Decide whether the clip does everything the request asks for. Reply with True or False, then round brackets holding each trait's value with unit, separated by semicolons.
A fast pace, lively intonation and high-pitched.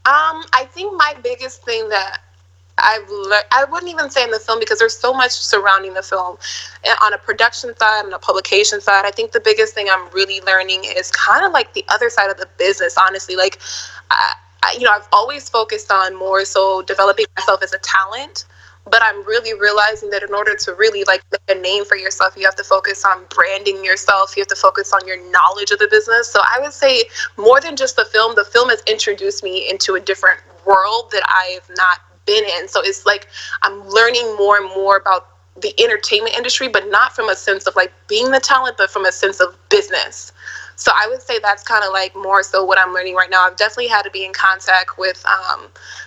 True (225 wpm; 6.2 semitones; 210 Hz)